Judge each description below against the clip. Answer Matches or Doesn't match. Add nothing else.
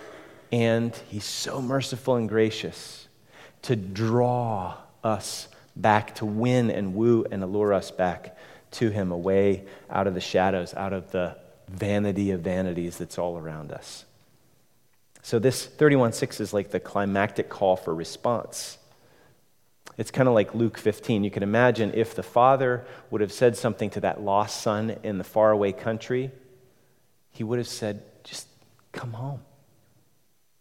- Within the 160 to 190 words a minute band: Doesn't match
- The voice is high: Doesn't match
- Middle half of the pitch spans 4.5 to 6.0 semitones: Doesn't match